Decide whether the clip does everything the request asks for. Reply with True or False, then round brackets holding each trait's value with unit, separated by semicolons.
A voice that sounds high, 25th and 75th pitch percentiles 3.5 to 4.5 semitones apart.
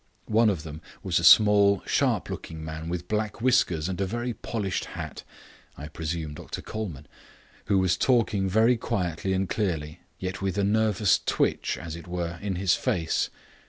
False (95 Hz; 4.0 semitones)